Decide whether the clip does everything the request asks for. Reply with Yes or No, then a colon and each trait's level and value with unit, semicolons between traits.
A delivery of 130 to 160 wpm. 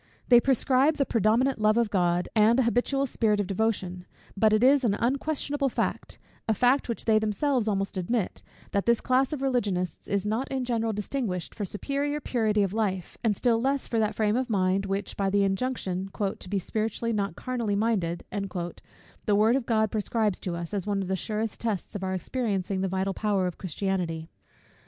No: average, 195 wpm